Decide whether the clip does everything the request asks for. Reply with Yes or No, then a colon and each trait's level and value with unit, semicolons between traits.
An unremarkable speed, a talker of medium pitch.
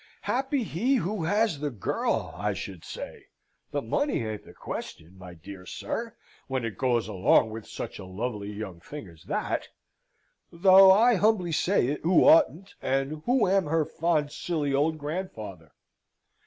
Yes: average, 160 wpm; medium, 150 Hz